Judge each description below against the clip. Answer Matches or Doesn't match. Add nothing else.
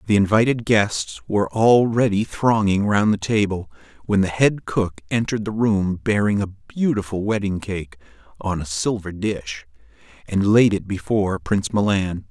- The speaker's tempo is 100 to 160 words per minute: Matches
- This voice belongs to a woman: Doesn't match